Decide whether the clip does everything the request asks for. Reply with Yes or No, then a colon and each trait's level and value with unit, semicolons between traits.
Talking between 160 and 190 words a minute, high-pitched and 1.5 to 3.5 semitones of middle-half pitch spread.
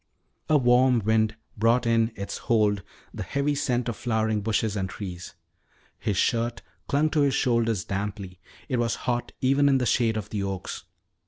No: average, 170 wpm; low, 115 Hz; average, 3.2 semitones